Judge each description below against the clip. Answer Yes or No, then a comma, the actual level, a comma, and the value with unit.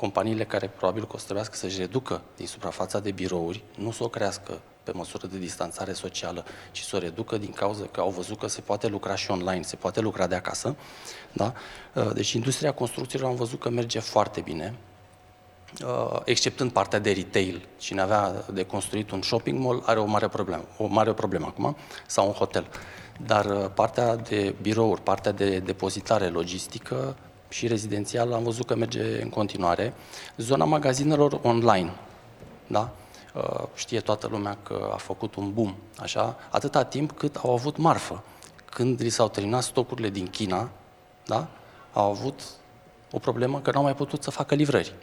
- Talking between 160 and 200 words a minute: Yes, fast, 170 wpm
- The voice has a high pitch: No, low, 110 Hz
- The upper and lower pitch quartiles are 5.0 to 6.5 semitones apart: No, average, 3.6 semitones